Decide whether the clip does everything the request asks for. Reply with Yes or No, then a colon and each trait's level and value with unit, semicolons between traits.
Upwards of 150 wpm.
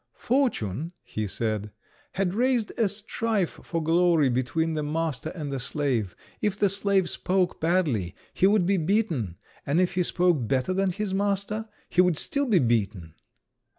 Yes: average, 160 wpm